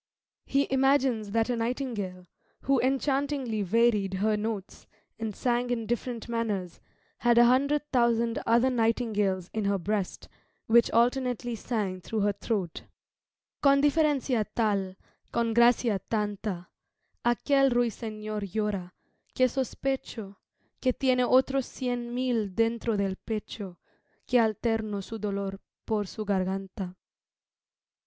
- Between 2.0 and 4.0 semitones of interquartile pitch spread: Yes, average, 3.4 semitones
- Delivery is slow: Yes, slow, 120 wpm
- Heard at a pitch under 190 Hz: No, high, 230 Hz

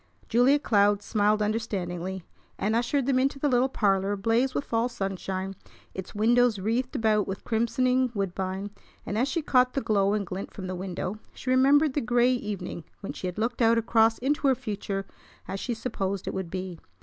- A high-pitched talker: Yes, high, 220 Hz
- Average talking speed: Yes, average, 185 wpm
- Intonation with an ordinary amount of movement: Yes, average, 4.2 semitones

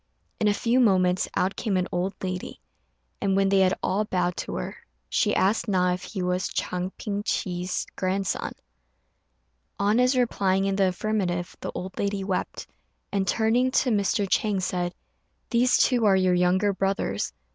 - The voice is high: Yes, high, 195 Hz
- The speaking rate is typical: Yes, average, 170 wpm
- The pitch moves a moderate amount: No, narrow, 2.3 semitones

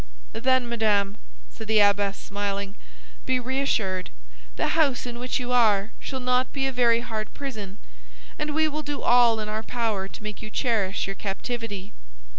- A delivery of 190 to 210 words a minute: No, average, 170 wpm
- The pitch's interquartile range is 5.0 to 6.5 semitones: No, average, 3.8 semitones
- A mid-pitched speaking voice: No, high, 230 Hz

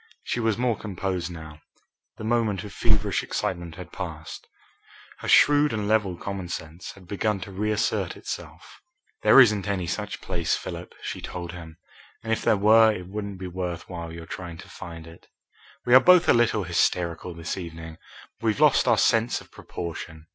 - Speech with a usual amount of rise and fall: Yes, average, 4.1 semitones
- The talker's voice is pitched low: Yes, very low, 95 Hz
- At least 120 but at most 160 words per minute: No, average, 175 wpm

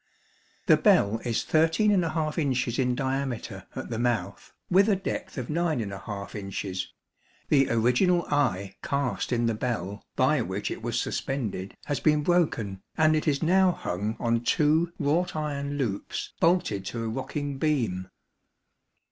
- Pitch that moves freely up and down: Yes, wide, 5.9 semitones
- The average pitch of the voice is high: No, low, 130 Hz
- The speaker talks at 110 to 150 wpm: Yes, average, 145 wpm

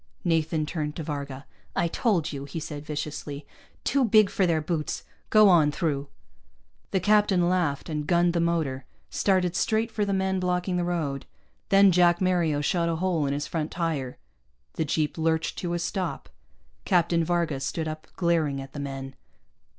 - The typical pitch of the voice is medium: Yes, medium, 165 Hz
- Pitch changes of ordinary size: Yes, average, 3.3 semitones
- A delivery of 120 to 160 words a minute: No, average, 175 wpm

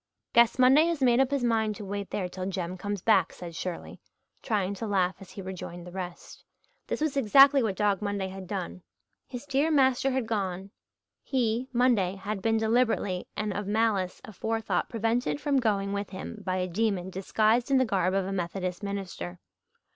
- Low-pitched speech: No, high, 205 Hz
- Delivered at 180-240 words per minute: Yes, average, 185 wpm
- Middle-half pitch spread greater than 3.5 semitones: Yes, average, 4.1 semitones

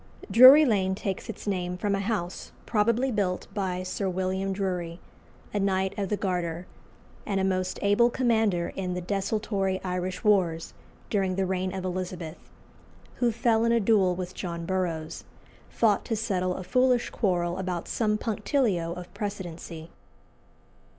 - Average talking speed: Yes, average, 150 wpm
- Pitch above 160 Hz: Yes, high, 190 Hz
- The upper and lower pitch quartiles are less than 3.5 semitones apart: Yes, narrow, 2.6 semitones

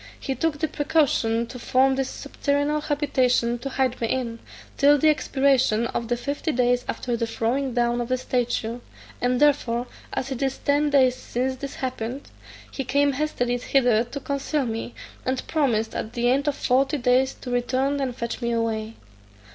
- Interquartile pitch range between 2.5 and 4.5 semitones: Yes, average, 2.8 semitones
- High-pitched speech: Yes, very high, 255 Hz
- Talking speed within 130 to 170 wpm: No, average, 180 wpm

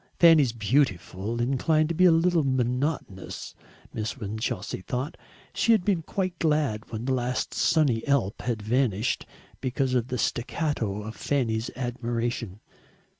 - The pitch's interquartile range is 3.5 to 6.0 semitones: Yes, average, 5.0 semitones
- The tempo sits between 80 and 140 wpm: Yes, slow, 135 wpm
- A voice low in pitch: Yes, low, 125 Hz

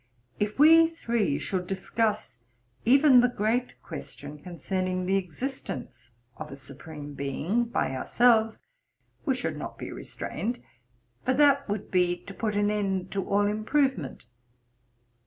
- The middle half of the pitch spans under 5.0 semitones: No, wide, 5.5 semitones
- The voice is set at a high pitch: Yes, high, 205 Hz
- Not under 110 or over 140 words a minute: Yes, slow, 135 wpm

